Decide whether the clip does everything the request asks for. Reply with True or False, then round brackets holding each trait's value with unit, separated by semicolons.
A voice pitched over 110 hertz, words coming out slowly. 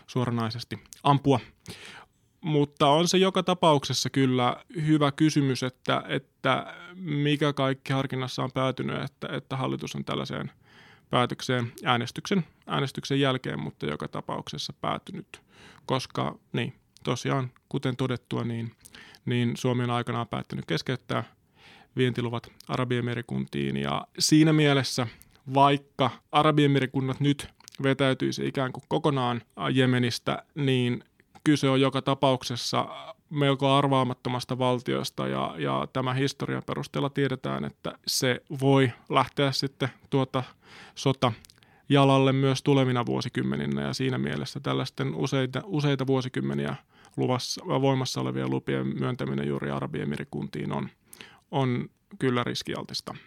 False (130 Hz; 110 wpm)